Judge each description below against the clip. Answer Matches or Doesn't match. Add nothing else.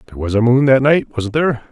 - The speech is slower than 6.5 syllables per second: Doesn't match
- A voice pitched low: Matches